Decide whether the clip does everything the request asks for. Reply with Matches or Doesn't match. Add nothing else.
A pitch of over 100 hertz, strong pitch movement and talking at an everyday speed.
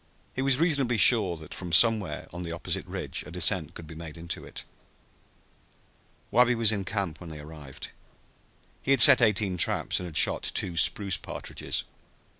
Doesn't match